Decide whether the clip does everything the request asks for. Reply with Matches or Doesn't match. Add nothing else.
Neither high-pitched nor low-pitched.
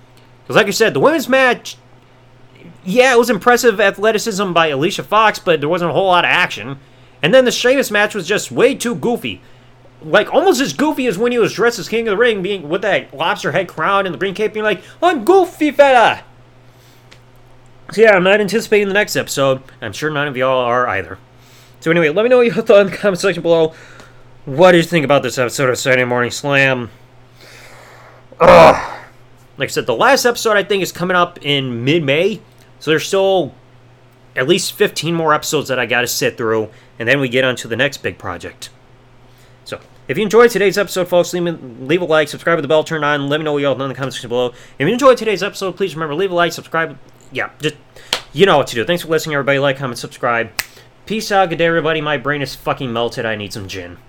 Matches